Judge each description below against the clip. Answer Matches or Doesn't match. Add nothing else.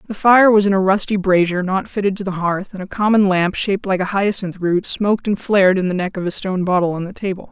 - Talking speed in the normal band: Doesn't match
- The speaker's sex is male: Doesn't match